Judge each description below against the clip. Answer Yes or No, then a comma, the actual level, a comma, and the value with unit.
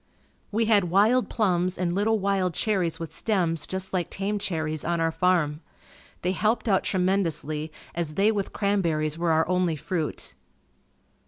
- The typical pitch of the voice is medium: Yes, medium, 180 Hz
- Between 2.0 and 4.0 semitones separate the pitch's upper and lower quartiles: Yes, average, 3.4 semitones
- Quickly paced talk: No, average, 155 wpm